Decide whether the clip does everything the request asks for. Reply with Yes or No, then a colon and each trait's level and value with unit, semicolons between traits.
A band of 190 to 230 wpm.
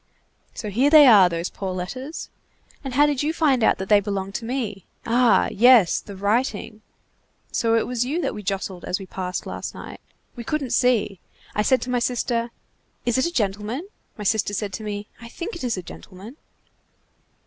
Yes: average, 195 wpm